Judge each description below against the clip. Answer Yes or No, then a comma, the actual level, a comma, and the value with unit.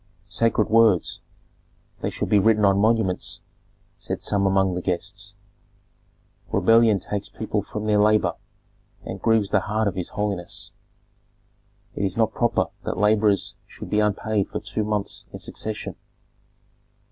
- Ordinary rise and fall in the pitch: No, narrow, 1.8 semitones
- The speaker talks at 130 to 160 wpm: Yes, average, 140 wpm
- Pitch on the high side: No, low, 105 Hz